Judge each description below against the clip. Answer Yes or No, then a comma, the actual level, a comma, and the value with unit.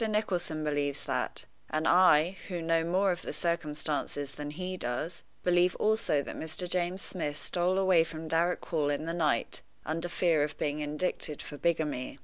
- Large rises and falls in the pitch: No, average, 3.1 semitones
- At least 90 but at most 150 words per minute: No, average, 170 wpm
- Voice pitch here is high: No, medium, 165 Hz